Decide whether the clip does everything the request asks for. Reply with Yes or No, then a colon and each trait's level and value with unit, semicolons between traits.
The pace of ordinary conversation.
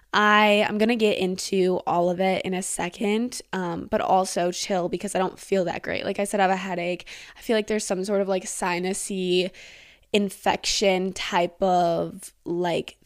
Yes: average, 190 wpm